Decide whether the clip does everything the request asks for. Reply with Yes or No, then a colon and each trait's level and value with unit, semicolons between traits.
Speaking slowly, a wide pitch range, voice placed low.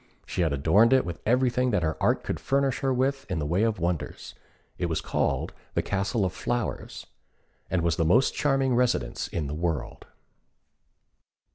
No: average, 175 wpm; wide, 7.1 semitones; low, 100 Hz